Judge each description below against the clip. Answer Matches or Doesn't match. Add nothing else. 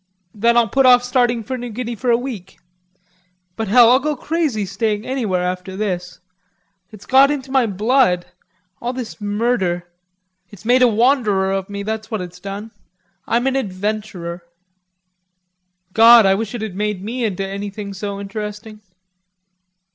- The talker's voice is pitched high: Matches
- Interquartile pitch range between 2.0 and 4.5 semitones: Matches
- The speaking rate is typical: Matches